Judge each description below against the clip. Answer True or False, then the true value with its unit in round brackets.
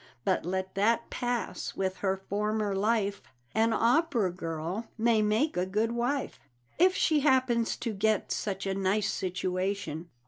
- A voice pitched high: True (210 Hz)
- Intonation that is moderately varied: True (3.6 semitones)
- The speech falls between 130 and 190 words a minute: True (145 wpm)